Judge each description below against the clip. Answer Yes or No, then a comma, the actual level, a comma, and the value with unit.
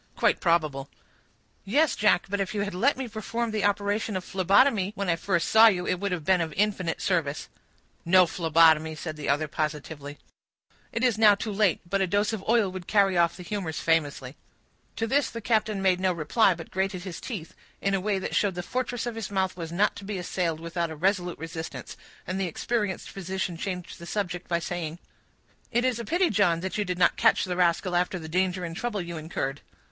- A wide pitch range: No, average, 3.6 semitones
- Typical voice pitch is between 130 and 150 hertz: No, medium, 185 Hz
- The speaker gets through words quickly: Yes, fast, 215 wpm